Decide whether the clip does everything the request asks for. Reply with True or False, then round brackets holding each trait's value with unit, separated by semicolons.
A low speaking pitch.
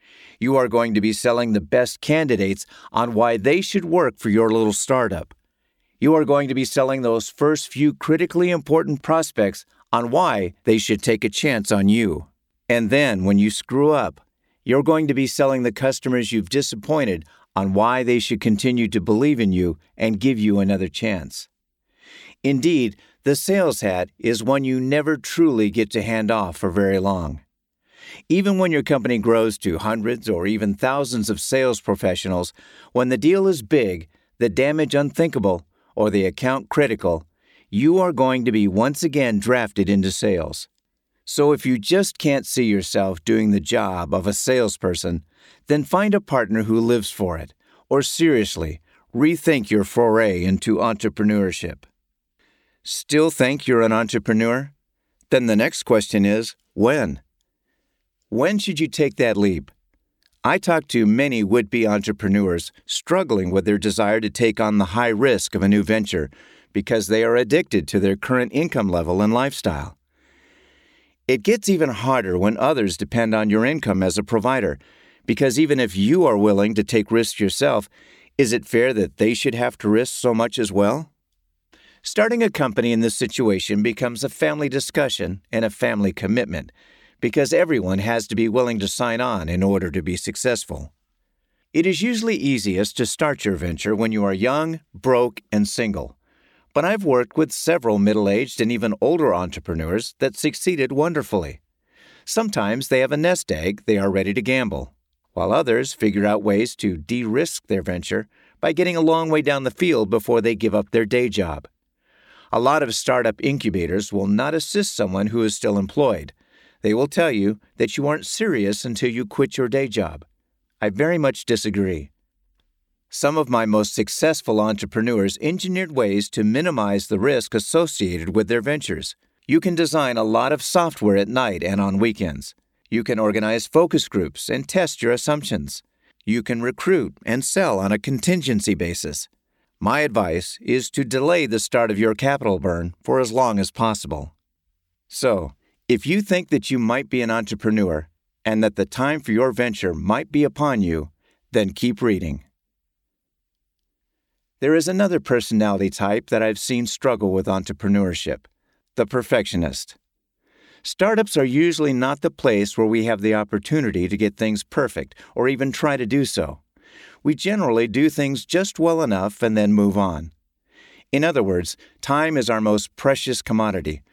True (115 Hz)